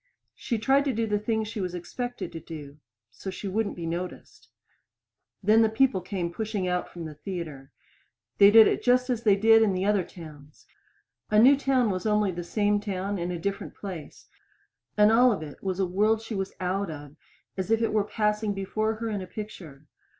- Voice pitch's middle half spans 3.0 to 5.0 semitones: Yes, average, 3.6 semitones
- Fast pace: Yes, fast, 210 wpm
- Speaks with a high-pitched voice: Yes, high, 200 Hz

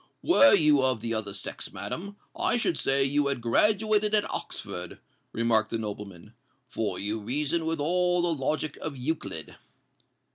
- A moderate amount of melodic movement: No, wide, 7.5 semitones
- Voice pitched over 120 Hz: Yes, medium, 140 Hz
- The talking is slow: No, average, 155 wpm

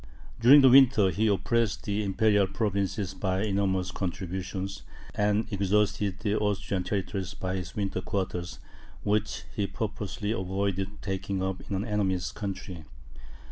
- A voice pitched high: No, low, 100 Hz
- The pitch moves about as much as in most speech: No, narrow, 1.9 semitones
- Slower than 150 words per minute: Yes, slow, 135 wpm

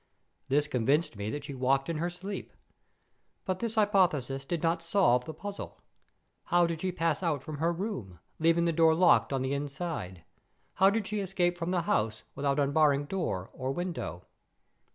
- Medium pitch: Yes, medium, 160 Hz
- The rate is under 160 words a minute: No, average, 175 wpm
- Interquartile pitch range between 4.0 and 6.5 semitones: Yes, average, 4.4 semitones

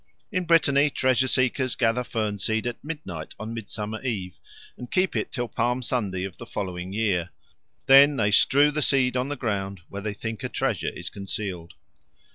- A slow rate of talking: No, average, 180 wpm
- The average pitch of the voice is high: No, low, 115 Hz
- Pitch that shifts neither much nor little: Yes, average, 4.8 semitones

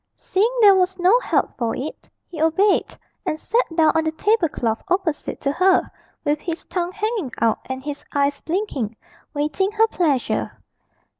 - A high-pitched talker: Yes, very high, 330 Hz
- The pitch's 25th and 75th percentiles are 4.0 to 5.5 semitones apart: Yes, average, 5.1 semitones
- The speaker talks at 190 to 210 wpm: No, average, 165 wpm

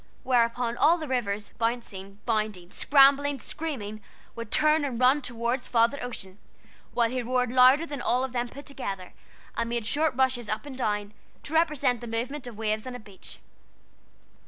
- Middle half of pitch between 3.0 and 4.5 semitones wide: Yes, average, 3.5 semitones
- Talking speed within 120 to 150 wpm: No, average, 170 wpm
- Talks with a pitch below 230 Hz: No, high, 245 Hz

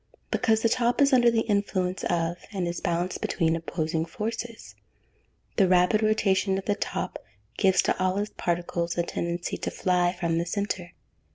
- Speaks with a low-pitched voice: No, medium, 185 Hz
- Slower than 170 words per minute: No, average, 175 wpm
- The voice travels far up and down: No, average, 3.7 semitones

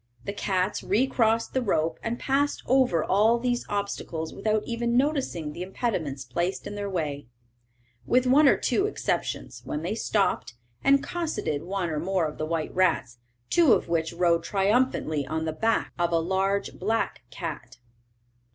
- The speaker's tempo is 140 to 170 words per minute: Yes, average, 165 wpm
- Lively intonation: Yes, wide, 6.3 semitones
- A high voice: Yes, high, 195 Hz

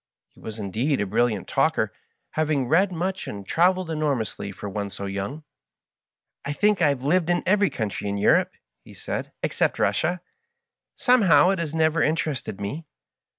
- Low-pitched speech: No, medium, 150 Hz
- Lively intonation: Yes, wide, 8.6 semitones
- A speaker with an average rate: Yes, average, 175 wpm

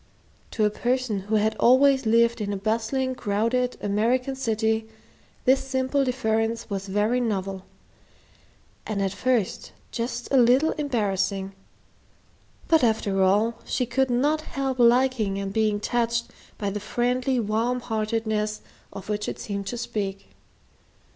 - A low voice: No, high, 225 Hz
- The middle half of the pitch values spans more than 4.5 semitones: No, average, 3.4 semitones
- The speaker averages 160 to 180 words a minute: No, slow, 135 wpm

